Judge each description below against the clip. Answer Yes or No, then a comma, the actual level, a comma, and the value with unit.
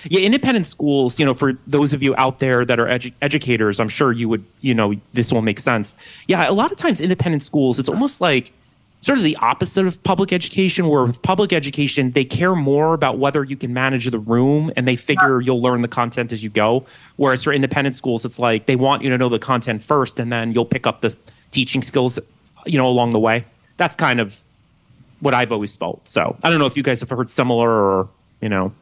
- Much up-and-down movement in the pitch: No, average, 3.8 semitones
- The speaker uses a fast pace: Yes, fast, 235 wpm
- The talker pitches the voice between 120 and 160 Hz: Yes, low, 130 Hz